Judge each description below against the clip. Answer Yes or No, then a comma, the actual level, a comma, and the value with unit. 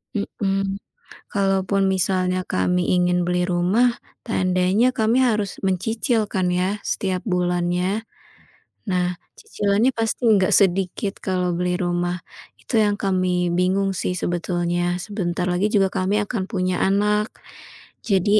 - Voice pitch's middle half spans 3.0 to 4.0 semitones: No, narrow, 2.4 semitones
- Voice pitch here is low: No, high, 190 Hz